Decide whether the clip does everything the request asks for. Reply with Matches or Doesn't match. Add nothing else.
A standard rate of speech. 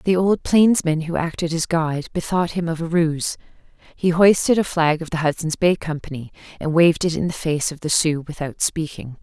Doesn't match